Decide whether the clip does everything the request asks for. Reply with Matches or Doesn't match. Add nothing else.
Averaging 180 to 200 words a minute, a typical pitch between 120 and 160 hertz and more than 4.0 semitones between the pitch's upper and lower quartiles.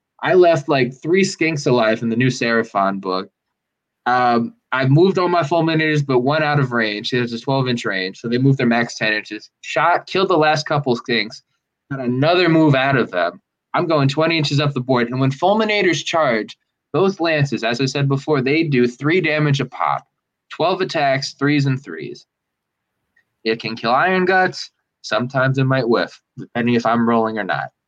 Matches